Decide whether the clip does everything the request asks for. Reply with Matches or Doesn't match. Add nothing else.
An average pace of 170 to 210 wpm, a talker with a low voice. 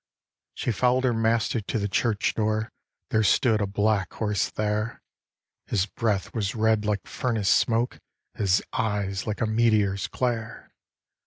Doesn't match